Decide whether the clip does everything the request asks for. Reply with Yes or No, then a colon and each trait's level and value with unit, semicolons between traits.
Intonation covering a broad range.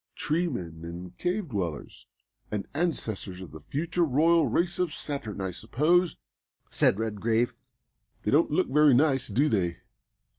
Yes: wide, 8.6 semitones